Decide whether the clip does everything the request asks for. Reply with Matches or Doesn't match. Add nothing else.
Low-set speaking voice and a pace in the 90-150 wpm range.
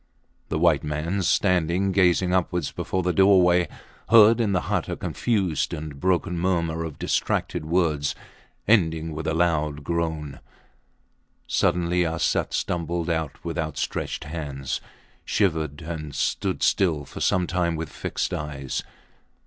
Matches